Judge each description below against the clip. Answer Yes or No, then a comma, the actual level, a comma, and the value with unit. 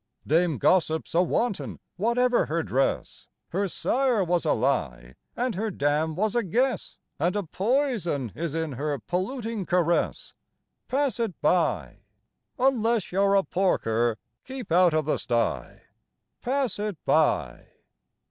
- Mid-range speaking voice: Yes, medium, 180 Hz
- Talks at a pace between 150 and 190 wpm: No, slow, 135 wpm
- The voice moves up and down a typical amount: No, wide, 6.9 semitones